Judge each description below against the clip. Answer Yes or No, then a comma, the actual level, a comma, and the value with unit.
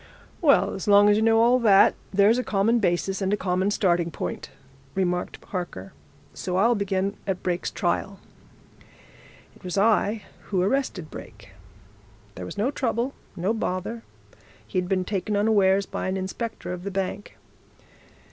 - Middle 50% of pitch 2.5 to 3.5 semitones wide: Yes, average, 3.1 semitones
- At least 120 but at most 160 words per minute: Yes, average, 155 wpm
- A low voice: No, high, 195 Hz